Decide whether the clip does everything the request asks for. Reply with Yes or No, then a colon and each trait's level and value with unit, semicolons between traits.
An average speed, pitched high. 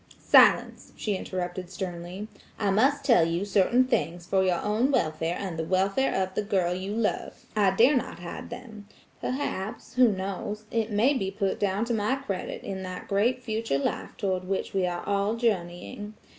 Yes: average, 170 wpm; high, 200 Hz